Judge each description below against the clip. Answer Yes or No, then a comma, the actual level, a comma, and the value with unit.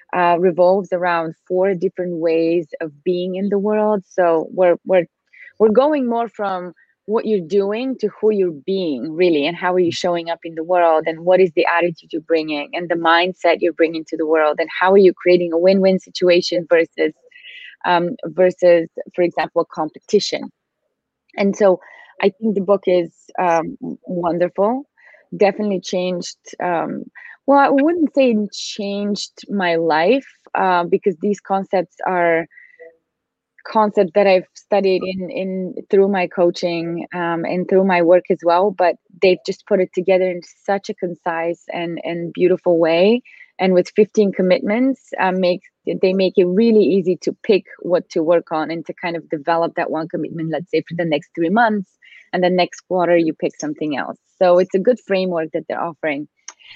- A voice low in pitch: No, medium, 180 Hz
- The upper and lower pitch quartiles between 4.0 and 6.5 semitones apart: No, average, 2.7 semitones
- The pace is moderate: Yes, average, 175 wpm